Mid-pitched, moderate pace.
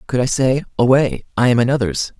No: low, 125 Hz; average, 190 wpm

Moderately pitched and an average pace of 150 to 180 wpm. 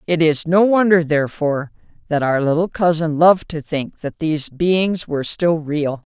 Yes: medium, 160 Hz; average, 175 wpm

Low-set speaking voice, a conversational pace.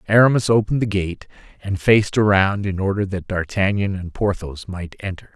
Yes: low, 100 Hz; average, 170 wpm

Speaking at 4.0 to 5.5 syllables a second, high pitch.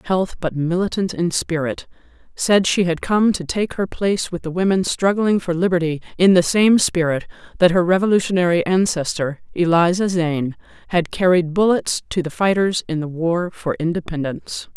No: 5.0 syllables/s; medium, 175 Hz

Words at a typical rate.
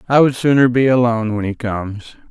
No: fast, 210 wpm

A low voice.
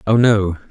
Yes: low, 100 Hz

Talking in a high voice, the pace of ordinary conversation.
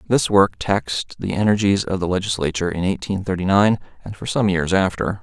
No: very low, 95 Hz; average, 195 wpm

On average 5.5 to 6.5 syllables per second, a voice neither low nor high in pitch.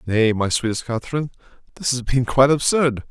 No: 6.0 syllables/s; low, 125 Hz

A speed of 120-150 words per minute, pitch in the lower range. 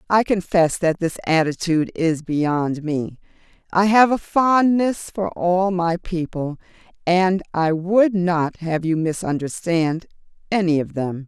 No: average, 140 wpm; medium, 175 Hz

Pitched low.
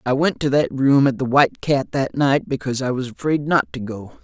Yes: low, 130 Hz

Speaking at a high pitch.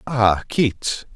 No: low, 115 Hz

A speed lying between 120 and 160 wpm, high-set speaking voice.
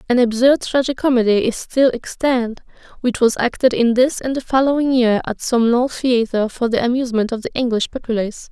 No: average, 185 wpm; high, 245 Hz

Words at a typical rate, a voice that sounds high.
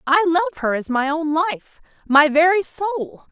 Yes: average, 165 wpm; very high, 315 Hz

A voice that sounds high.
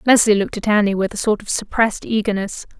Yes: high, 205 Hz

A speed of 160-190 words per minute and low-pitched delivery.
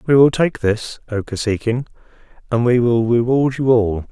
Yes: average, 175 wpm; low, 120 Hz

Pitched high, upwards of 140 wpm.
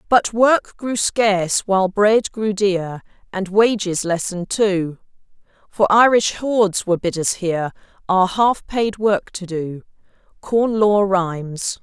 No: high, 200 Hz; slow, 135 wpm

